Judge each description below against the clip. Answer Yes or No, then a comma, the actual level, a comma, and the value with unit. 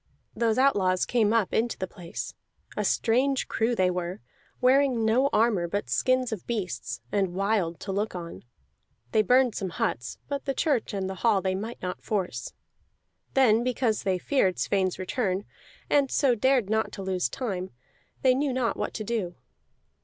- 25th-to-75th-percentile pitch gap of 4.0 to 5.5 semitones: Yes, average, 4.9 semitones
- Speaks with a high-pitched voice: Yes, high, 215 Hz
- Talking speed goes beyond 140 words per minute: Yes, average, 170 wpm